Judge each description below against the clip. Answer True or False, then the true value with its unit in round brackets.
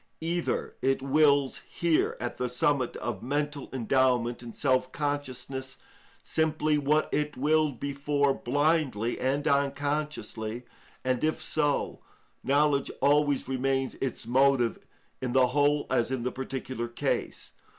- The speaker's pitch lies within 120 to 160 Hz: True (135 Hz)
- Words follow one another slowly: True (125 wpm)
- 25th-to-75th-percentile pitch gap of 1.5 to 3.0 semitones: True (2.5 semitones)